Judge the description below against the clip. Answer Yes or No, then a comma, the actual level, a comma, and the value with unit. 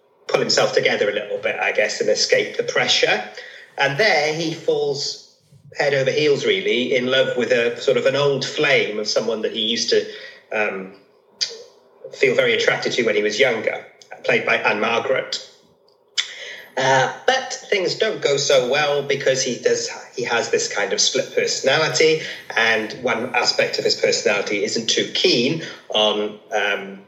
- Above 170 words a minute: No, average, 165 wpm